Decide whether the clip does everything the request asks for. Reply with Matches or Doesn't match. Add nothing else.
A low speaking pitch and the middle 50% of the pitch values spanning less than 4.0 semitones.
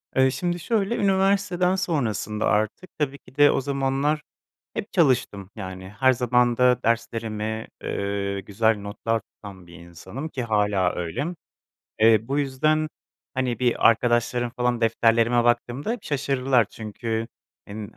Doesn't match